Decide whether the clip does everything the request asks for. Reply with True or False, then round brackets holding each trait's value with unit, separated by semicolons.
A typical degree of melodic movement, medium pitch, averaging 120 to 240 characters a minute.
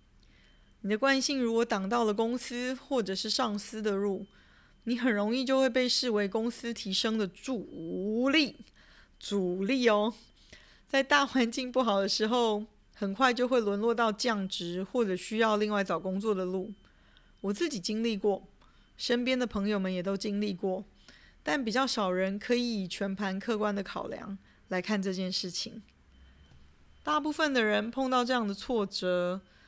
False (3.9 semitones; 215 Hz; 235 characters per minute)